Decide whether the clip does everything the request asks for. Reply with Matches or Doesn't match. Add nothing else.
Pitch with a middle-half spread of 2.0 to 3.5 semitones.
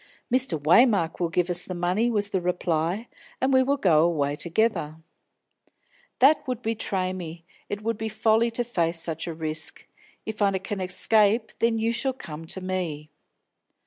Doesn't match